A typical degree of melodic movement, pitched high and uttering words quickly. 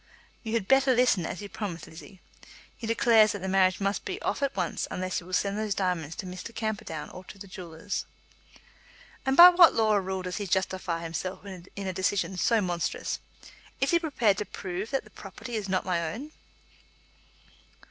No: average, 3.2 semitones; high, 195 Hz; average, 195 wpm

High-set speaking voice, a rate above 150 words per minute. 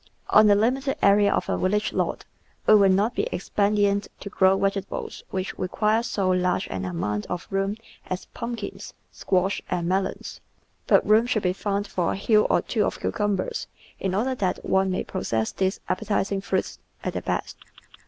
Yes: high, 200 Hz; average, 175 wpm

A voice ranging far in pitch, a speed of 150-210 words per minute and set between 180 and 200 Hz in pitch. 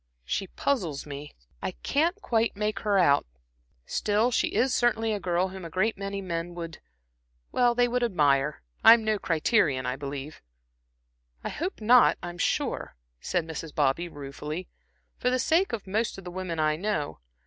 Yes: wide, 6.5 semitones; average, 160 wpm; medium, 185 Hz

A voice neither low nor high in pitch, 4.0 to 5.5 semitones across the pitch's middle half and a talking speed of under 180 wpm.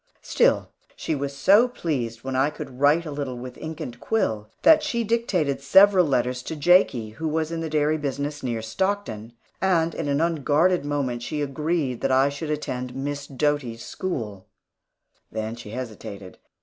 Yes: medium, 145 Hz; average, 4.6 semitones; average, 170 wpm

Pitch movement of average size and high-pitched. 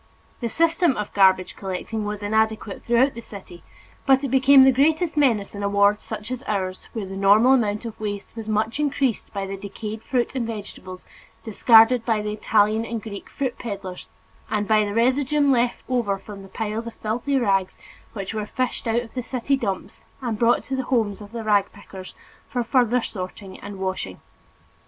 Yes: average, 3.6 semitones; high, 220 Hz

